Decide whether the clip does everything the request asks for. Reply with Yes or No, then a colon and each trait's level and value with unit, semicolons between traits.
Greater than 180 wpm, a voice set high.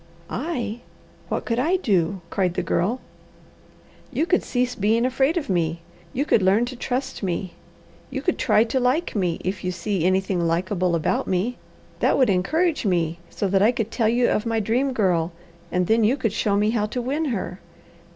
Yes: average, 190 wpm; high, 215 Hz